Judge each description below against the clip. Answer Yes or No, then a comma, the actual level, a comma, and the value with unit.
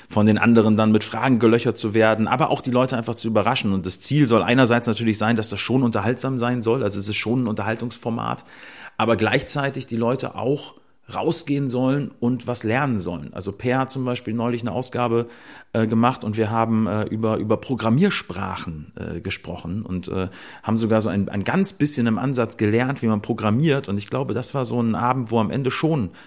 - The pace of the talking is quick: Yes, fast, 210 wpm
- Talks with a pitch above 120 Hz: No, low, 115 Hz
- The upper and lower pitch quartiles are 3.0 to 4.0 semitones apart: No, narrow, 2.6 semitones